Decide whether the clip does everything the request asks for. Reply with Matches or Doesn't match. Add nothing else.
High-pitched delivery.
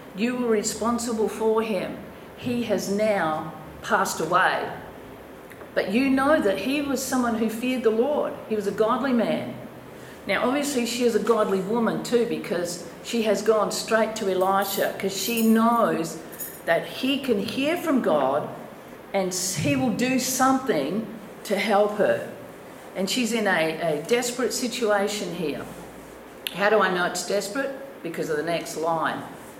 Matches